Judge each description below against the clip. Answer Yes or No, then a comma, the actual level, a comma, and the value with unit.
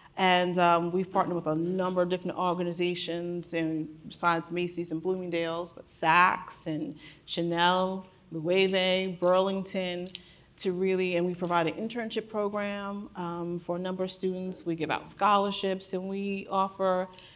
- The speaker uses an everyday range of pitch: No, narrow, 1.7 semitones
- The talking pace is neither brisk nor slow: Yes, average, 145 wpm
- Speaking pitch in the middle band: Yes, medium, 180 Hz